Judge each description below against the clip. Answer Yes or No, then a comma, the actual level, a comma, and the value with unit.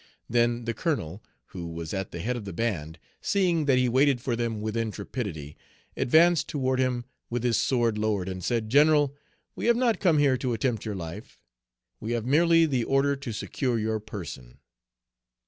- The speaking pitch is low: Yes, low, 120 Hz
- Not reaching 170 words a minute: No, average, 180 wpm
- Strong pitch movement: No, average, 4.7 semitones